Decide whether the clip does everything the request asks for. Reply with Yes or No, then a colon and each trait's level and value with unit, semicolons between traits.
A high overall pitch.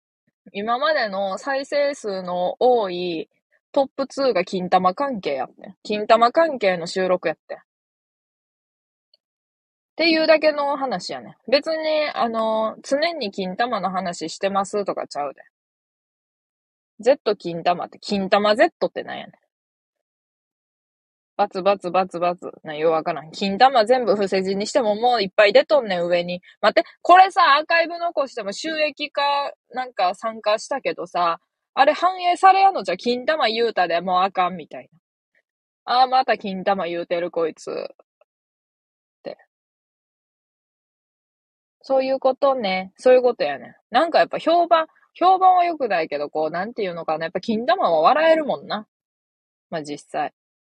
Yes: high, 225 Hz